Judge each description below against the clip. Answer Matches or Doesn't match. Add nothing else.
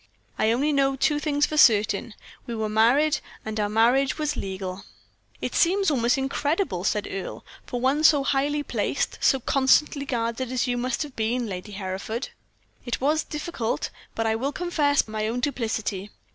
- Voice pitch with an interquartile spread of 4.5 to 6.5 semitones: Matches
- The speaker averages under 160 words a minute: Doesn't match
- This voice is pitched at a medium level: Doesn't match